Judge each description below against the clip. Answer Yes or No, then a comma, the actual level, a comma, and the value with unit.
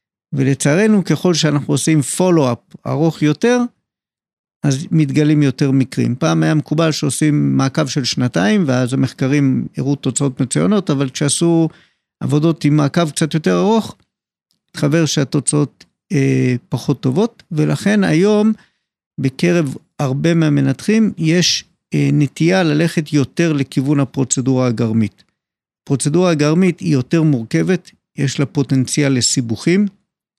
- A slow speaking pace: No, average, 115 wpm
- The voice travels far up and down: No, average, 3.8 semitones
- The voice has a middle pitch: Yes, medium, 150 Hz